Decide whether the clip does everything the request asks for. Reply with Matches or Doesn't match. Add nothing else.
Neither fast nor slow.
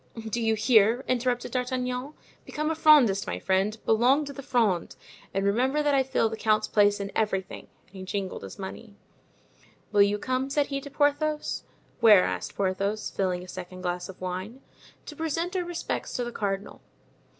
Matches